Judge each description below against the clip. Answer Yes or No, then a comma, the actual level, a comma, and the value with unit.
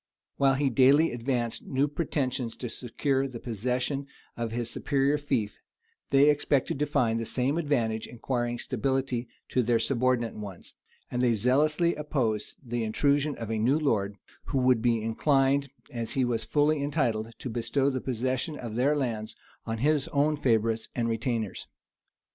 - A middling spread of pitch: Yes, average, 3.4 semitones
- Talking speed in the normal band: Yes, average, 160 wpm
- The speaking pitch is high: No, low, 125 Hz